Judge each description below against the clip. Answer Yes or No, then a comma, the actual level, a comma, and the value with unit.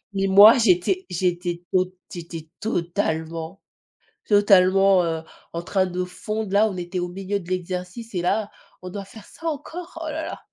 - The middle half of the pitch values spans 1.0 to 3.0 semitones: Yes, average, 2.7 semitones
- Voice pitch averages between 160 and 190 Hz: Yes, medium, 185 Hz